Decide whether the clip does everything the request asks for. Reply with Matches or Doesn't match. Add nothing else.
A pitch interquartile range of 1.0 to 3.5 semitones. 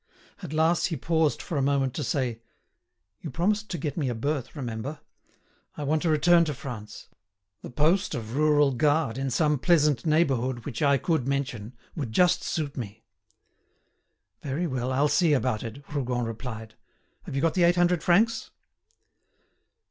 Doesn't match